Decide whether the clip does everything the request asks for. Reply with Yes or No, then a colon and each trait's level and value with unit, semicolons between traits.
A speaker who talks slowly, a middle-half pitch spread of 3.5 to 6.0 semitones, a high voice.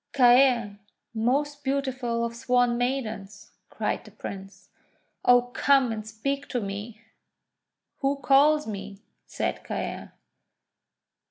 Yes: slow, 105 wpm; average, 3.9 semitones; high, 245 Hz